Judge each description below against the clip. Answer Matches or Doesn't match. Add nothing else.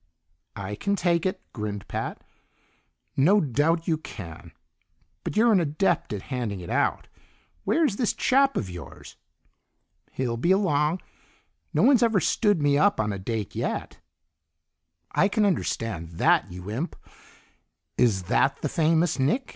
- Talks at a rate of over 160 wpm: Doesn't match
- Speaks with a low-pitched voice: Doesn't match